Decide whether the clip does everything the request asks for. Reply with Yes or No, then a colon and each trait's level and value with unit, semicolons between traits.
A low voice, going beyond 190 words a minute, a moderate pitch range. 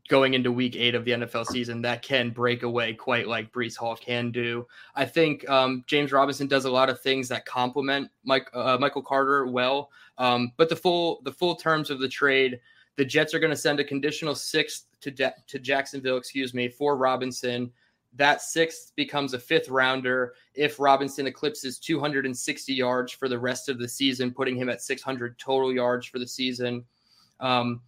No: low, 130 Hz; average, 200 wpm; narrow, 2.2 semitones